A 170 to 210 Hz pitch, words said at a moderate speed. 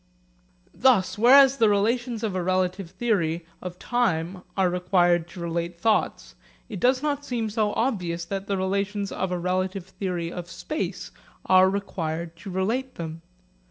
Yes: high, 190 Hz; average, 155 wpm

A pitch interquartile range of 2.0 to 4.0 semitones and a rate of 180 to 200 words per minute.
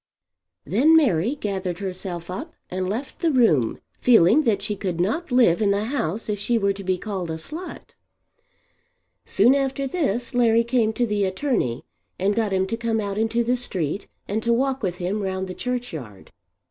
No: average, 4.7 semitones; average, 185 wpm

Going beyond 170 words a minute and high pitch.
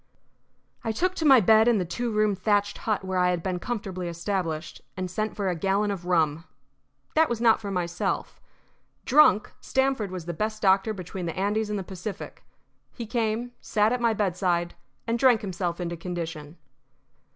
Yes: average, 180 wpm; high, 195 Hz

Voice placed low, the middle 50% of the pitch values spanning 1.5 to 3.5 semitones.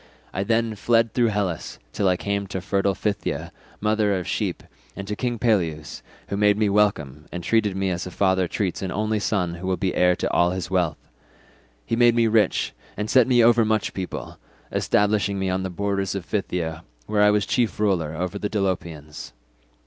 Yes: low, 100 Hz; average, 2.8 semitones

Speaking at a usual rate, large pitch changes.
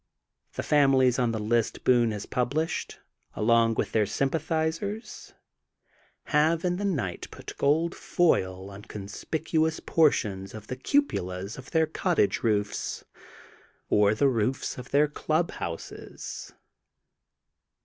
No: slow, 120 wpm; wide, 7.0 semitones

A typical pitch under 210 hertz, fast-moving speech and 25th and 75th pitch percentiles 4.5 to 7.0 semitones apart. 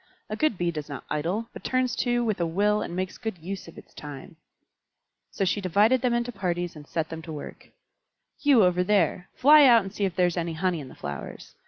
Yes: medium, 185 Hz; fast, 230 wpm; average, 5.1 semitones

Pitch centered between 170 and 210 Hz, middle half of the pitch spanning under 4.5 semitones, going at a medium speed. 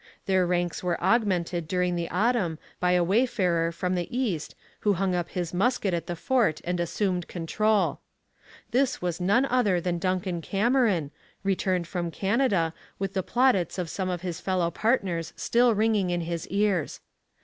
Yes: medium, 185 Hz; average, 3.3 semitones; average, 165 wpm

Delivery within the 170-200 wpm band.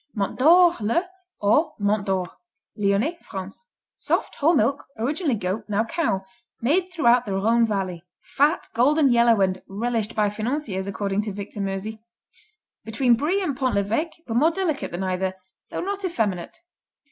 No: average, 155 wpm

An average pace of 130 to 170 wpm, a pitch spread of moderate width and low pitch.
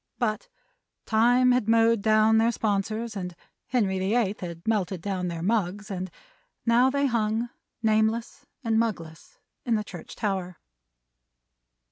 No: slow, 135 wpm; average, 3.3 semitones; high, 215 Hz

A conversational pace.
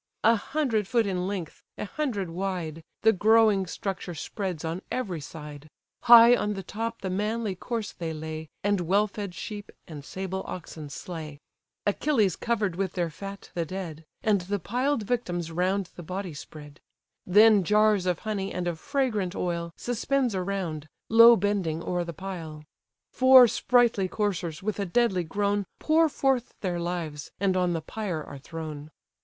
Yes: average, 160 wpm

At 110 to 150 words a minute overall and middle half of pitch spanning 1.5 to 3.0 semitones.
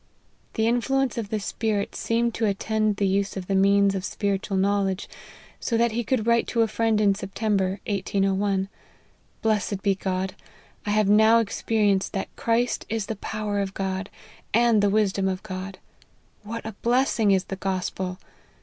No: average, 175 wpm; narrow, 2.4 semitones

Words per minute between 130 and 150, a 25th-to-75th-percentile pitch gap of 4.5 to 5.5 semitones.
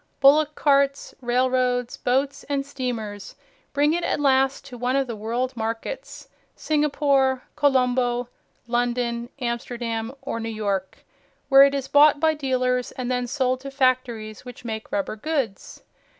No: average, 140 wpm; narrow, 2.6 semitones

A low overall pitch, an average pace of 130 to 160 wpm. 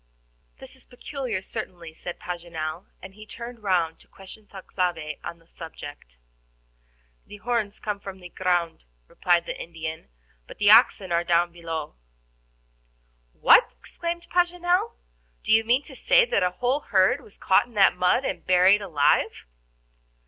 No: medium, 185 Hz; average, 155 wpm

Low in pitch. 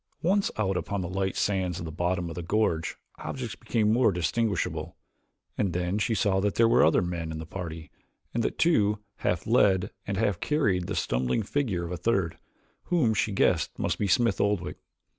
Yes: very low, 95 Hz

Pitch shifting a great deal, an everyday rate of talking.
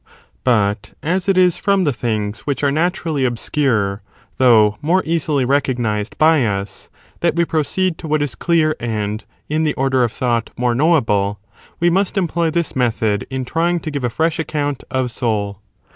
Yes: wide, 6.2 semitones; average, 175 wpm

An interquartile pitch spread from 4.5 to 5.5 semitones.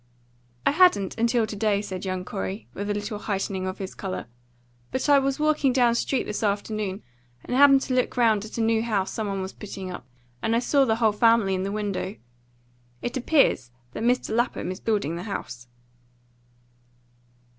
No: average, 3.8 semitones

